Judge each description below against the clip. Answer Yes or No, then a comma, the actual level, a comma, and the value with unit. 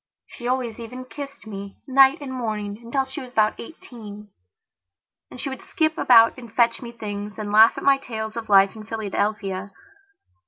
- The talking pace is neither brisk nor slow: Yes, average, 180 wpm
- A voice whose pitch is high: Yes, high, 230 Hz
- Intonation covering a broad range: No, average, 3.5 semitones